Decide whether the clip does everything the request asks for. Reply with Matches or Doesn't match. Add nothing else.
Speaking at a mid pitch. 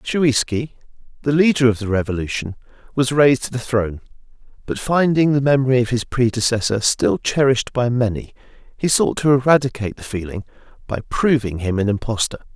Doesn't match